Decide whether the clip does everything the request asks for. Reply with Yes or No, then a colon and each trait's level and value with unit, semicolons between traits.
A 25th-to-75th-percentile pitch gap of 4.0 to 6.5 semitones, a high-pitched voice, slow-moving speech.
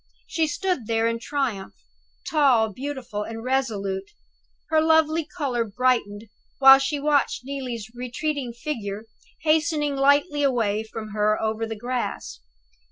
Yes: average, 4.7 semitones; very high, 250 Hz; slow, 125 wpm